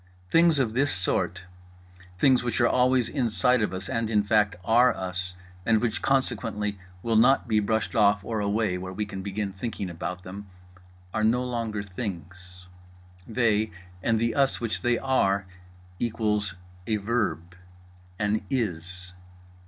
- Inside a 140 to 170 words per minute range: Yes, average, 145 wpm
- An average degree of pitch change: Yes, average, 4.1 semitones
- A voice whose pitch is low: Yes, low, 105 Hz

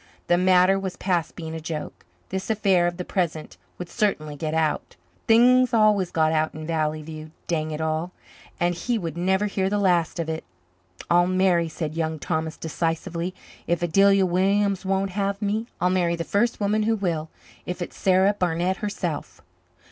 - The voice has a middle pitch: Yes, medium, 180 Hz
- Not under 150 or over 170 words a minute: No, average, 180 wpm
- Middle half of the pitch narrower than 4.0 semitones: Yes, average, 3.4 semitones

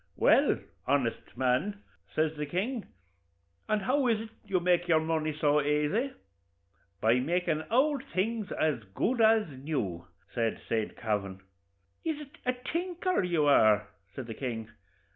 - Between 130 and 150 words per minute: Yes, average, 145 wpm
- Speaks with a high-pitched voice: No, medium, 160 Hz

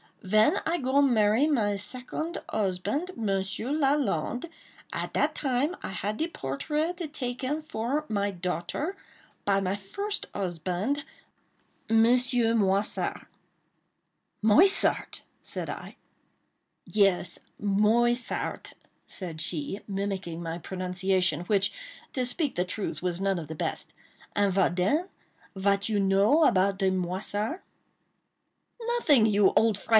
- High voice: Yes, high, 205 Hz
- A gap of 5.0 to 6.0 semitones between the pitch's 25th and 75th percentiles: Yes, average, 5.3 semitones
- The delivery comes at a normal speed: No, slow, 115 wpm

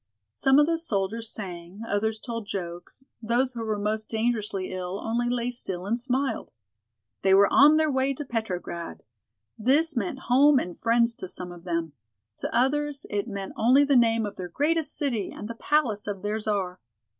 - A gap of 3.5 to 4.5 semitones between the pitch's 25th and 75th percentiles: No, average, 5.0 semitones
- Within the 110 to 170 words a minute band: No, average, 180 wpm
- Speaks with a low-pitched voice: No, high, 225 Hz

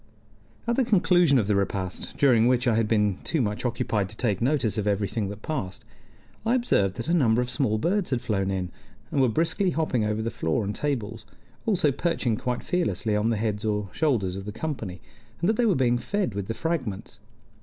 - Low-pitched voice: Yes, low, 115 Hz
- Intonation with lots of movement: Yes, wide, 6.7 semitones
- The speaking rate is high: Yes, fast, 210 wpm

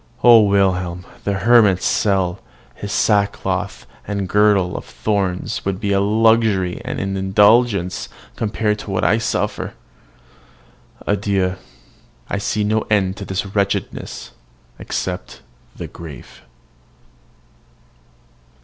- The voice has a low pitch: Yes, low, 100 Hz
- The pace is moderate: No, slow, 105 wpm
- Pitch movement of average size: No, narrow, 1.9 semitones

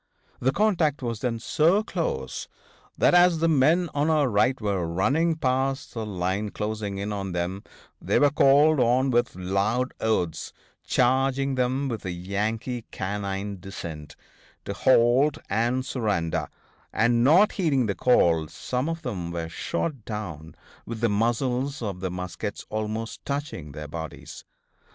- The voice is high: No, low, 115 Hz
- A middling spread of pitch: No, wide, 5.7 semitones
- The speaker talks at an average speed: Yes, average, 145 wpm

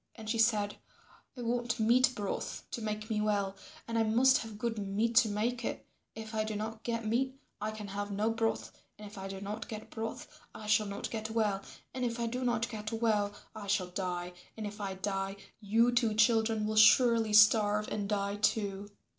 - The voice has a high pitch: Yes, high, 215 Hz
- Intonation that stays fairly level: Yes, narrow, 1.9 semitones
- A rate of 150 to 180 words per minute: No, fast, 205 wpm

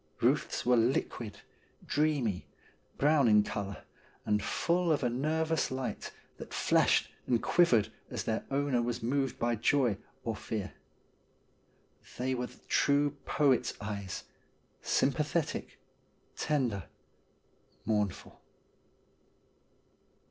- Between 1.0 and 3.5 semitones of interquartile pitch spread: No, average, 4.7 semitones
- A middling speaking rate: No, slow, 105 wpm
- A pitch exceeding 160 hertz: No, low, 125 Hz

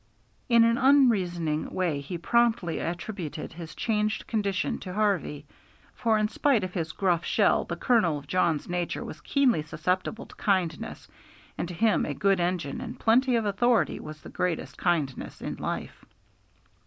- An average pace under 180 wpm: Yes, average, 160 wpm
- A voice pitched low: No, medium, 185 Hz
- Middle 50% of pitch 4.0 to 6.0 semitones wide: Yes, average, 5.1 semitones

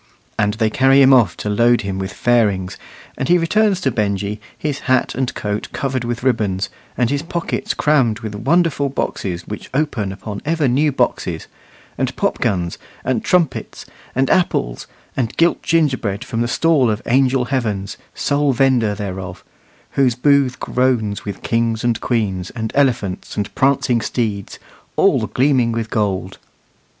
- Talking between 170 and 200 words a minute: No, average, 155 wpm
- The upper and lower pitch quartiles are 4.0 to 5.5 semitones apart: Yes, average, 4.7 semitones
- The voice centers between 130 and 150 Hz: No, low, 120 Hz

